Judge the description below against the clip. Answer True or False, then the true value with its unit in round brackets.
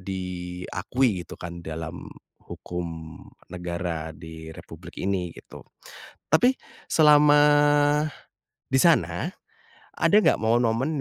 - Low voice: True (95 Hz)